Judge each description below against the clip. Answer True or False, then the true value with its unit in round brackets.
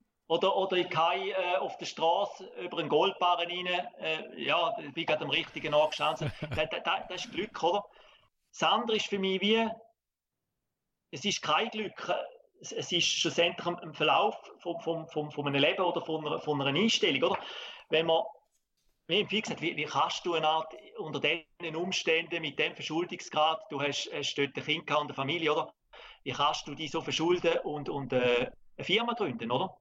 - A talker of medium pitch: True (165 Hz)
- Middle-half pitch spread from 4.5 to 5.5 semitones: False (3.0 semitones)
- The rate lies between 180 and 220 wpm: True (185 wpm)